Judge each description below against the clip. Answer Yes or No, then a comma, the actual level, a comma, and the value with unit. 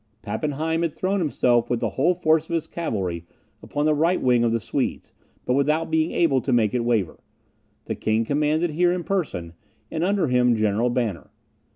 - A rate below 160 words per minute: No, average, 190 wpm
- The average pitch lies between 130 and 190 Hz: Yes, medium, 140 Hz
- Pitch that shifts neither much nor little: No, wide, 5.7 semitones